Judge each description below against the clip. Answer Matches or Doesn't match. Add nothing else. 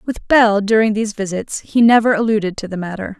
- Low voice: Doesn't match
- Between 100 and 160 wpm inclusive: Doesn't match